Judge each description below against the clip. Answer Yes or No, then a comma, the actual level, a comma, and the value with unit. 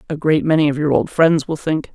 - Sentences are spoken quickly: Yes, fast, 280 wpm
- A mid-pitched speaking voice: Yes, medium, 150 Hz